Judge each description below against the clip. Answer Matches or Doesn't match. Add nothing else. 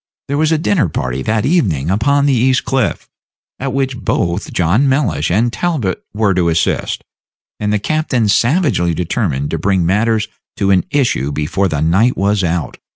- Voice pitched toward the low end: Matches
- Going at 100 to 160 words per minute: Doesn't match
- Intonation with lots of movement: Matches